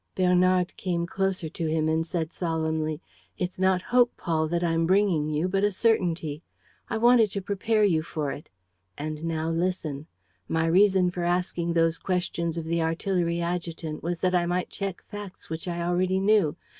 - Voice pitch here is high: No, medium, 175 Hz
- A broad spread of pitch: No, narrow, 2.4 semitones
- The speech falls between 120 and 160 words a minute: No, average, 175 wpm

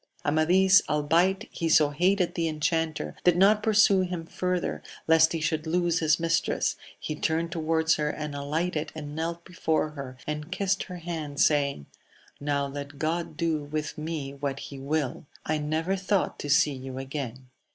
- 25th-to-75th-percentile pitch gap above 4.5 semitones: No, average, 2.8 semitones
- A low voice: No, medium, 155 Hz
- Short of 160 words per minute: No, average, 165 wpm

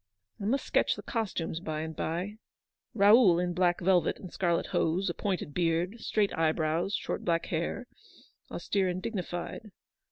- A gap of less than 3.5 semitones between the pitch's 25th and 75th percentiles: Yes, average, 3.1 semitones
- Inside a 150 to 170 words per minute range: Yes, average, 165 wpm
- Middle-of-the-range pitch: Yes, medium, 180 Hz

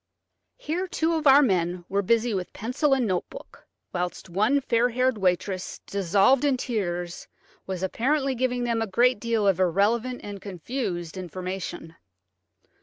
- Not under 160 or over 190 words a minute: No, average, 150 wpm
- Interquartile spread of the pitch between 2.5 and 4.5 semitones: No, wide, 5.5 semitones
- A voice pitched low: No, high, 215 Hz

